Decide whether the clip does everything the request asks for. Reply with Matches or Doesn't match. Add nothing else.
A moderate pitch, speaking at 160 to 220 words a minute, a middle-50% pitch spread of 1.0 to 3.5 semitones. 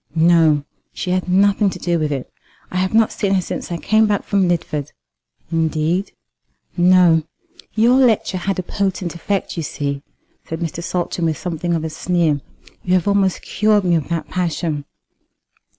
Matches